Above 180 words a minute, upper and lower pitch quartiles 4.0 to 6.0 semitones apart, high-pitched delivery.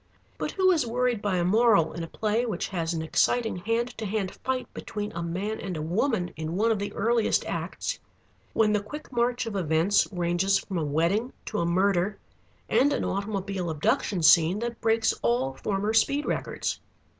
Yes: average, 190 wpm; average, 4.7 semitones; high, 200 Hz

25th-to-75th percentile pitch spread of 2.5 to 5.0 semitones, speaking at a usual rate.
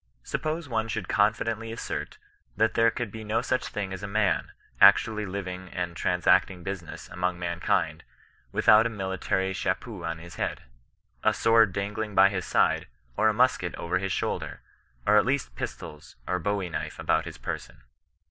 Yes: average, 3.5 semitones; average, 175 wpm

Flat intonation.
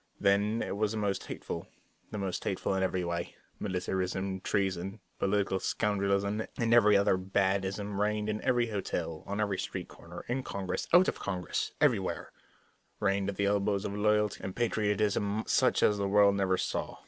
Yes: narrow, 1.7 semitones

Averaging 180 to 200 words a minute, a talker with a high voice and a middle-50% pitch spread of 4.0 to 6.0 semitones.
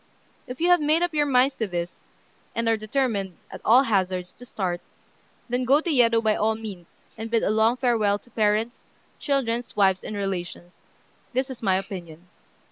Yes: average, 185 wpm; high, 225 Hz; average, 4.4 semitones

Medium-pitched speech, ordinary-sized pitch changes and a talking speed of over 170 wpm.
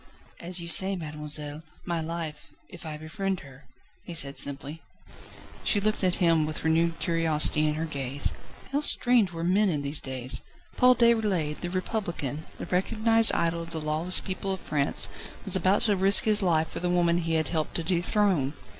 Yes: medium, 170 Hz; average, 3.8 semitones; average, 180 wpm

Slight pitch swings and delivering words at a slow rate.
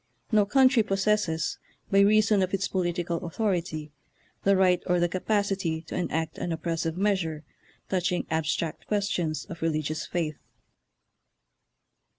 No: average, 3.6 semitones; slow, 130 wpm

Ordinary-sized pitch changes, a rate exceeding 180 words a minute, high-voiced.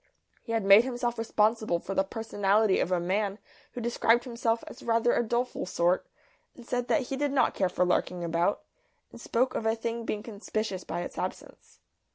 Yes: average, 3.6 semitones; average, 190 wpm; high, 225 Hz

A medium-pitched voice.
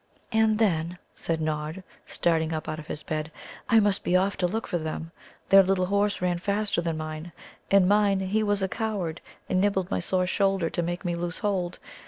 Yes: medium, 180 Hz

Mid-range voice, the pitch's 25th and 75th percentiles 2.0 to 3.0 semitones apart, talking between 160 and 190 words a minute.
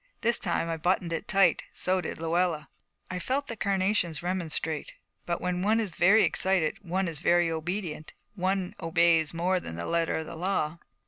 Yes: medium, 175 Hz; narrow, 2.5 semitones; average, 180 wpm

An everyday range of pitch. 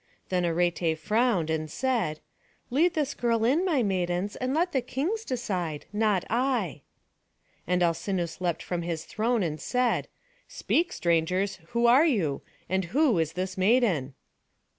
No: wide, 6.6 semitones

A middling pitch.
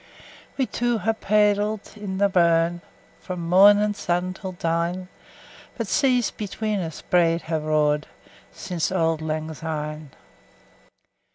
Yes: medium, 180 Hz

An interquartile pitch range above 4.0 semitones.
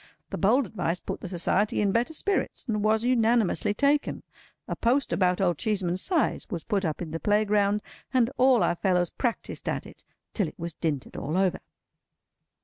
Yes: average, 4.7 semitones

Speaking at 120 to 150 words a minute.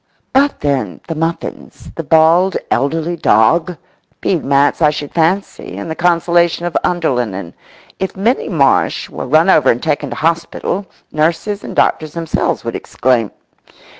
Yes: average, 140 wpm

